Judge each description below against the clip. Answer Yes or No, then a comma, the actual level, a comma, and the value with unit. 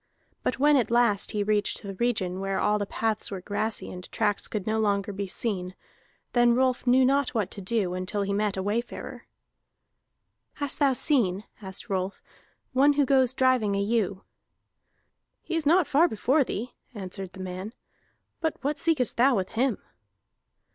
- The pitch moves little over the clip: No, average, 4.6 semitones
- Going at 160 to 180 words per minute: Yes, average, 170 wpm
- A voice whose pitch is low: No, high, 220 Hz